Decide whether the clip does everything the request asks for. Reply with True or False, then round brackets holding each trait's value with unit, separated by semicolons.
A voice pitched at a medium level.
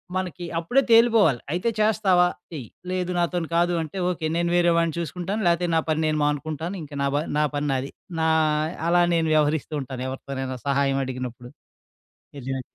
True (160 Hz)